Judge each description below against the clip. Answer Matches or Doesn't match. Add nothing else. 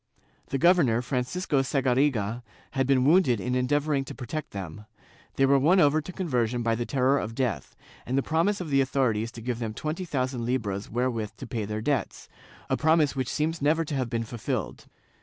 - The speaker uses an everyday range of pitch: Matches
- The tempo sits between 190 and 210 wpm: Matches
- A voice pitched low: Matches